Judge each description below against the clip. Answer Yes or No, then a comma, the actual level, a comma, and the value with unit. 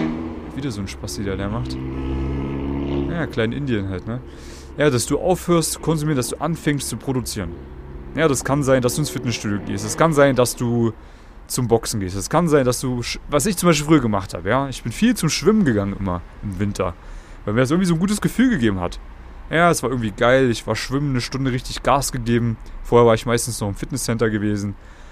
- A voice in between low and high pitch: No, low, 120 Hz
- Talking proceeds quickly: Yes, fast, 225 wpm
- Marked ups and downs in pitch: Yes, wide, 6.1 semitones